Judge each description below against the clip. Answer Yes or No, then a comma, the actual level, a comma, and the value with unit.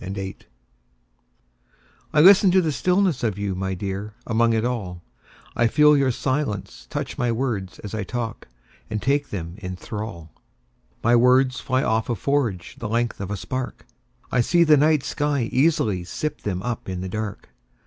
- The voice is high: No, low, 115 Hz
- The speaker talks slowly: No, average, 150 wpm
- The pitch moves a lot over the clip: Yes, wide, 5.9 semitones